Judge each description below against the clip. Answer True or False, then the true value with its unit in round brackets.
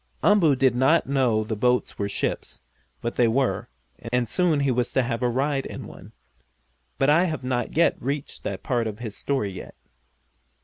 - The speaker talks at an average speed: True (180 wpm)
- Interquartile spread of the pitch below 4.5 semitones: True (3.2 semitones)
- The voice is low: True (125 Hz)